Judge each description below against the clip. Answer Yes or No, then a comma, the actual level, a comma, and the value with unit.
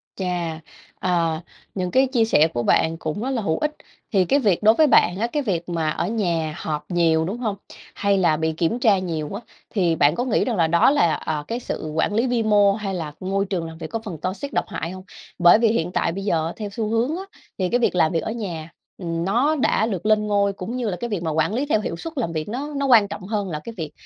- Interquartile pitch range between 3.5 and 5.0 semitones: No, wide, 5.4 semitones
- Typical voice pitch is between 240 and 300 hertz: No, high, 195 Hz